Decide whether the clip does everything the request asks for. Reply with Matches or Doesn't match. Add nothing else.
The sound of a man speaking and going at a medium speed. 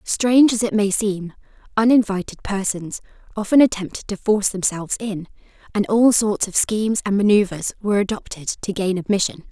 Doesn't match